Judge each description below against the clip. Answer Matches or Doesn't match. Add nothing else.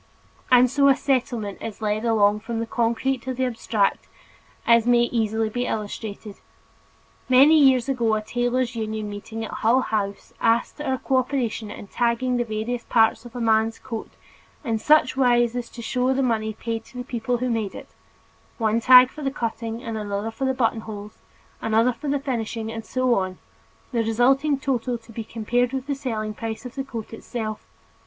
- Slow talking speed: Doesn't match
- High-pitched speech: Matches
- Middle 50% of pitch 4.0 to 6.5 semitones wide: Doesn't match